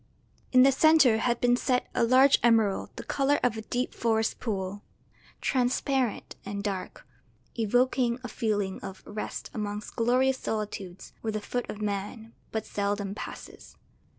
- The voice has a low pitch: No, high, 225 Hz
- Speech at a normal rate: Yes, average, 150 wpm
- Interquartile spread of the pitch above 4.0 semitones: No, average, 3.5 semitones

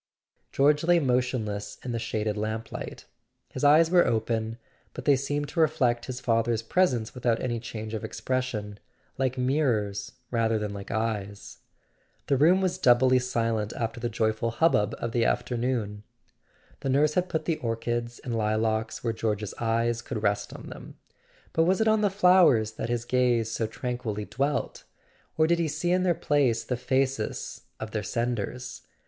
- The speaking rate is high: No, average, 165 wpm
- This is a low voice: Yes, low, 120 Hz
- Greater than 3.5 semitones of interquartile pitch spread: Yes, average, 4.0 semitones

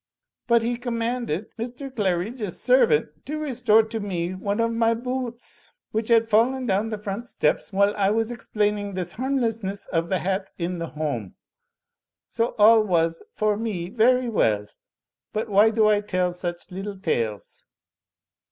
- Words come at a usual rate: Yes, average, 160 wpm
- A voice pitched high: Yes, high, 210 Hz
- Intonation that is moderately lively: Yes, average, 3.8 semitones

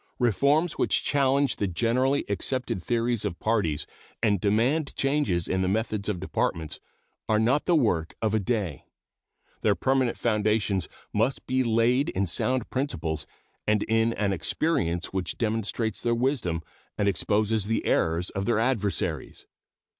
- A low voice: Yes, low, 110 Hz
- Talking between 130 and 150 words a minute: Yes, average, 145 wpm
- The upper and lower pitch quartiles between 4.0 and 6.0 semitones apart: Yes, average, 4.5 semitones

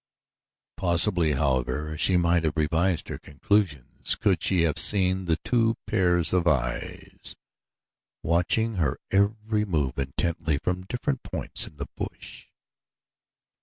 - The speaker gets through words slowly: Yes, slow, 125 wpm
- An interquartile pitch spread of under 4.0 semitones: No, average, 4.3 semitones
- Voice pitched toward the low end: Yes, very low, 85 Hz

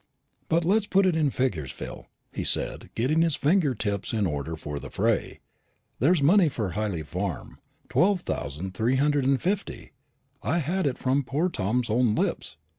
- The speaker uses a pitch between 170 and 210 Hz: No, low, 130 Hz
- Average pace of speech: Yes, average, 180 wpm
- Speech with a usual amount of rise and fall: No, wide, 8.5 semitones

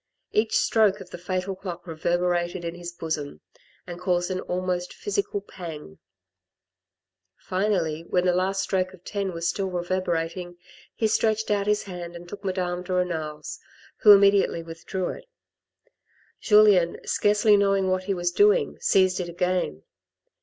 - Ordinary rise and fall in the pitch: No, narrow, 2.2 semitones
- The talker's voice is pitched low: No, medium, 185 Hz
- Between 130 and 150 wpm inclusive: Yes, average, 145 wpm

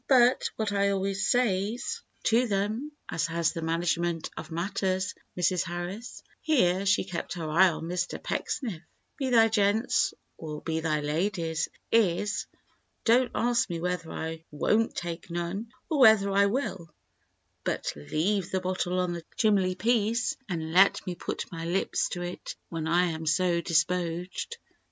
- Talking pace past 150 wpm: No, average, 145 wpm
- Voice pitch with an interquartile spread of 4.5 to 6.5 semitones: No, average, 3.9 semitones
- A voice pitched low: No, medium, 185 Hz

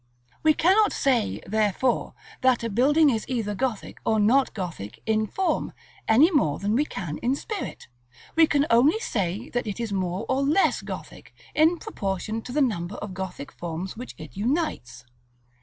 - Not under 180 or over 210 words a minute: No, average, 170 wpm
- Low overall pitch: No, high, 230 Hz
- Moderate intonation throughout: No, wide, 6.4 semitones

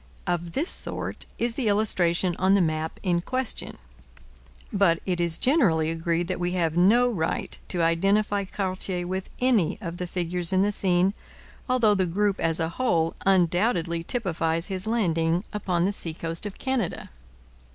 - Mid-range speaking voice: Yes, medium, 180 Hz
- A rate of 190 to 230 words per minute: No, average, 160 wpm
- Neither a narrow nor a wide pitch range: Yes, average, 3.5 semitones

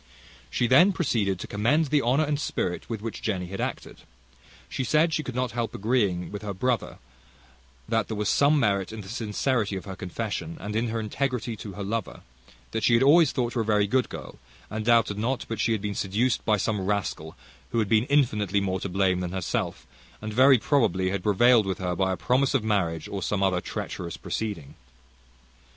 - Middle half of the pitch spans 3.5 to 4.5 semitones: Yes, average, 4.1 semitones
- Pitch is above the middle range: No, low, 110 Hz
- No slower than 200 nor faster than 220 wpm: Yes, fast, 205 wpm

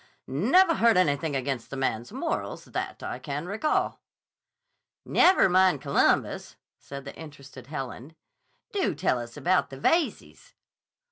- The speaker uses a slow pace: Yes, slow, 130 wpm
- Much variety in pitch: Yes, wide, 5.8 semitones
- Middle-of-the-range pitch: Yes, medium, 145 Hz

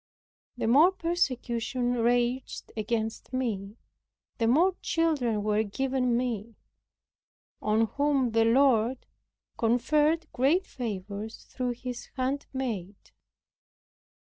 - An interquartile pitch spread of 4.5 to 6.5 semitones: No, average, 3.2 semitones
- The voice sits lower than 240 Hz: No, high, 245 Hz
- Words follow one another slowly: Yes, slow, 90 wpm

